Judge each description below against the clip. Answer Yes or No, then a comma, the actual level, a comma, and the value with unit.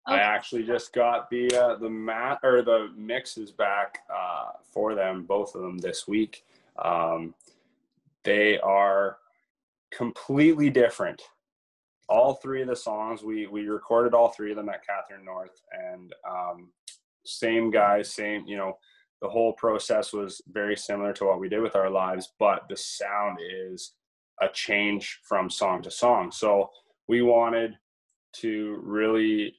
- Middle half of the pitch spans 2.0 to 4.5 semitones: Yes, average, 2.9 semitones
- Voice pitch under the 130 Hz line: Yes, low, 105 Hz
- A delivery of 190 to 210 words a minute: No, average, 150 wpm